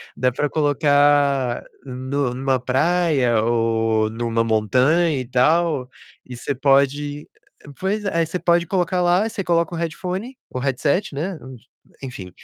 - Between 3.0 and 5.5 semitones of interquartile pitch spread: Yes, average, 5.2 semitones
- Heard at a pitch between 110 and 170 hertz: Yes, medium, 140 Hz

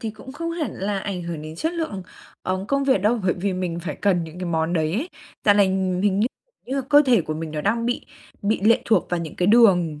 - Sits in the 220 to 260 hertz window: No, high, 195 Hz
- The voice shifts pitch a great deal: No, average, 5.0 semitones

